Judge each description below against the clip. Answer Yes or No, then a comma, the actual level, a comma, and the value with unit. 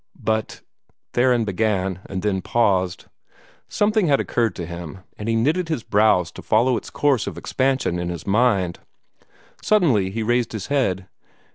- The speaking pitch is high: No, low, 110 Hz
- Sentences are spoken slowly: No, average, 160 wpm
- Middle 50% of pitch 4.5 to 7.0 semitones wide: Yes, average, 5.2 semitones